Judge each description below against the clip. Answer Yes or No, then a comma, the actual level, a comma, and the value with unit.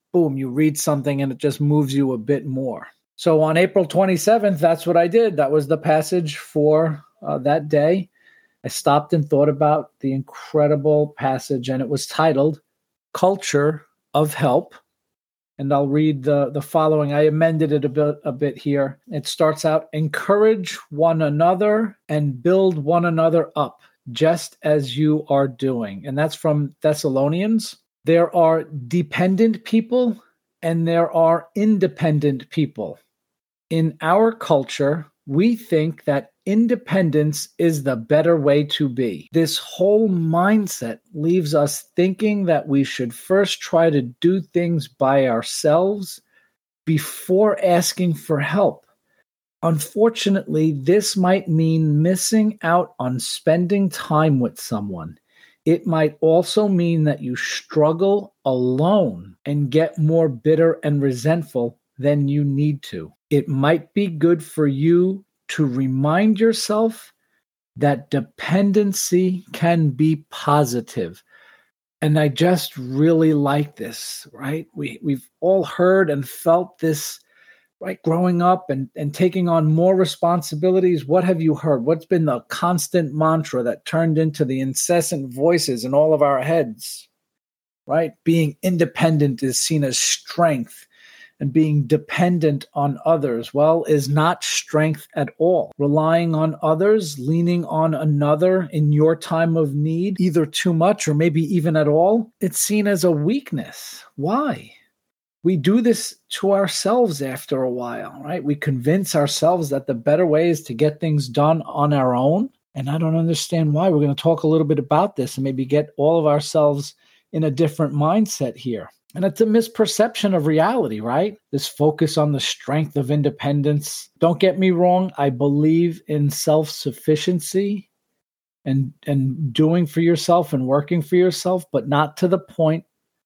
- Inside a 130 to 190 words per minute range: Yes, average, 150 wpm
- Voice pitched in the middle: Yes, medium, 160 Hz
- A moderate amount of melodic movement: Yes, average, 3.4 semitones